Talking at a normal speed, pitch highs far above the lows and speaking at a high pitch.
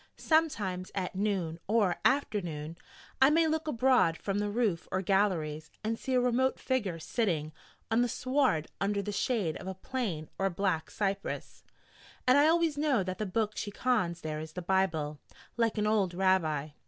Yes: average, 170 wpm; wide, 5.9 semitones; high, 200 Hz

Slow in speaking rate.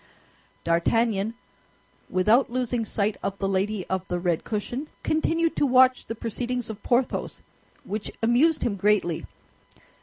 Yes: slow, 130 wpm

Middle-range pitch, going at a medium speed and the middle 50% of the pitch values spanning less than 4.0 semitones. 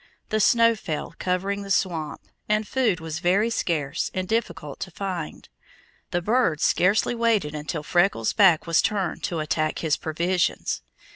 No: medium, 180 Hz; average, 150 wpm; average, 4.6 semitones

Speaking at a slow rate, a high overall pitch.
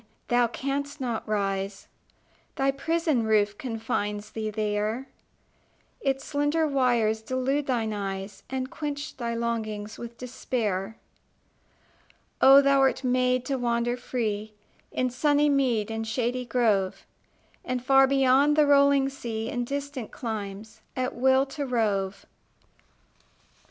Yes: slow, 120 wpm; high, 245 Hz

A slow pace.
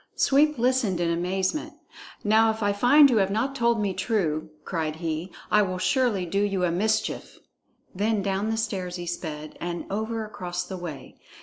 No: average, 180 wpm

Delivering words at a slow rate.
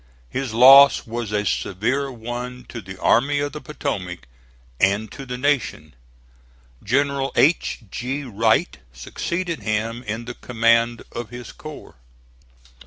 Yes: slow, 130 wpm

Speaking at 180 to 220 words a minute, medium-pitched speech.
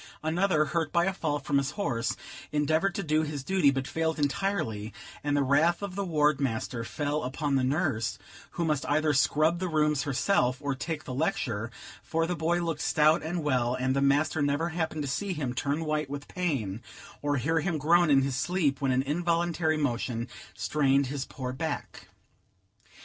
Yes: average, 190 wpm; medium, 150 Hz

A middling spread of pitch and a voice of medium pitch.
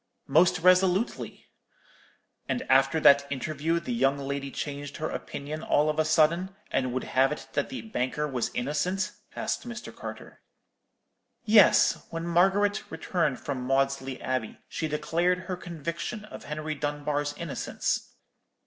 Yes: average, 4.3 semitones; medium, 155 Hz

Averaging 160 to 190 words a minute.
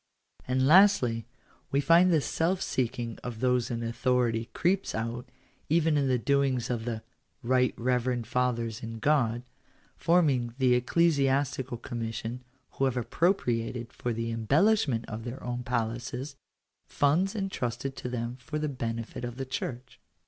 No: average, 150 wpm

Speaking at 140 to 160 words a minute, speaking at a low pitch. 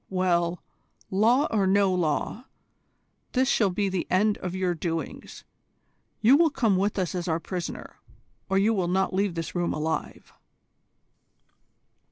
No: average, 145 wpm; high, 190 Hz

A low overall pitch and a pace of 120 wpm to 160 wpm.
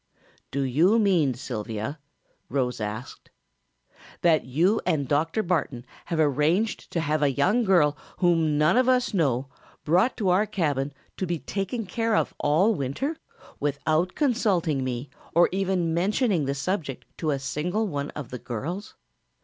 No: medium, 160 Hz; average, 150 wpm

